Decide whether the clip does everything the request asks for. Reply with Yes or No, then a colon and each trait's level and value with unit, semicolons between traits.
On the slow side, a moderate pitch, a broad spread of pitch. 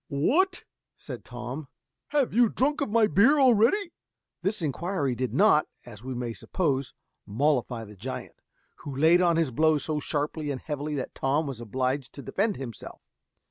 No: average, 170 wpm; medium, 150 Hz; wide, 7.3 semitones